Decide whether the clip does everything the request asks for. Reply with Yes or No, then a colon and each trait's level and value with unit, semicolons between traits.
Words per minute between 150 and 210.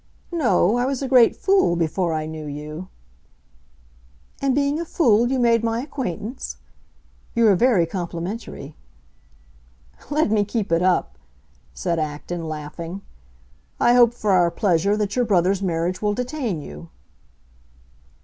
No: average, 140 wpm